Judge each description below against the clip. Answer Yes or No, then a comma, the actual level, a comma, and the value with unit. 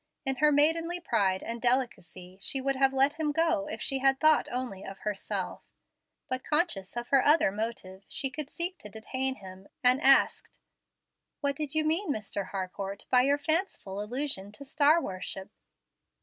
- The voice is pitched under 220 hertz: No, very high, 265 Hz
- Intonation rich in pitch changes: Yes, wide, 6.8 semitones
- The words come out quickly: No, average, 170 wpm